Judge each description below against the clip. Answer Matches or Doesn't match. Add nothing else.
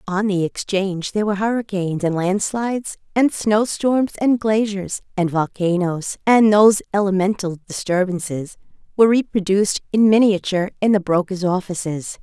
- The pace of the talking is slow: Matches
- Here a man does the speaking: Doesn't match